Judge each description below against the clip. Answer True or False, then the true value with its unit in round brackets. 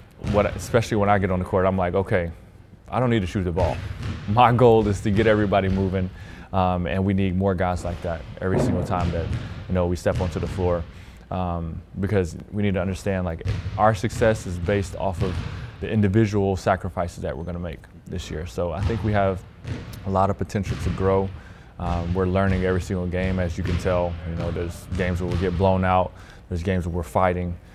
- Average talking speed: False (220 wpm)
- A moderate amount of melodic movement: False (2.2 semitones)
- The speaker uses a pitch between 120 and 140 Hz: False (95 Hz)